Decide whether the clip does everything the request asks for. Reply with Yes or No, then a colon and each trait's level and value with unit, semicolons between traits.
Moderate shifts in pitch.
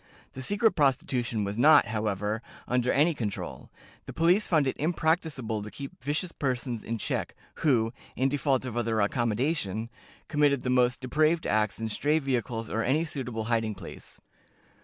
Yes: average, 4.8 semitones